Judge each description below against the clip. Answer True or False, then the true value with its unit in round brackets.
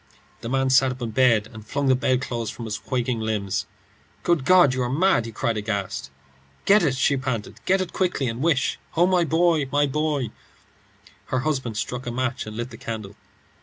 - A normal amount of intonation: True (4.2 semitones)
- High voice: False (130 Hz)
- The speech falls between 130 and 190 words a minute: False (200 wpm)